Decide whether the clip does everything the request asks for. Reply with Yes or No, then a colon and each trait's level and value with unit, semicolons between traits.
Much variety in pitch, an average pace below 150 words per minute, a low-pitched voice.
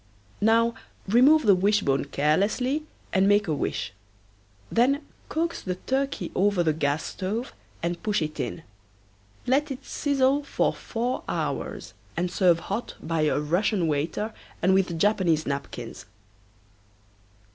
No: wide, 7.1 semitones; slow, 135 wpm; high, 200 Hz